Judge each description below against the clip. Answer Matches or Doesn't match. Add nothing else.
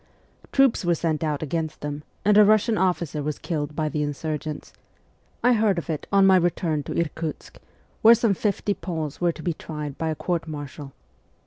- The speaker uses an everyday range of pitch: Matches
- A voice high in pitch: Doesn't match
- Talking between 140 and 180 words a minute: Doesn't match